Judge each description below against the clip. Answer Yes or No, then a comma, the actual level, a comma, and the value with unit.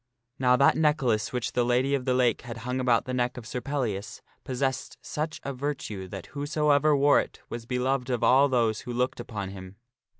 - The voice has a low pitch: Yes, low, 125 Hz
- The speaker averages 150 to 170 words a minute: No, fast, 205 wpm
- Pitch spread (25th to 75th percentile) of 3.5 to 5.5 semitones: No, average, 2.7 semitones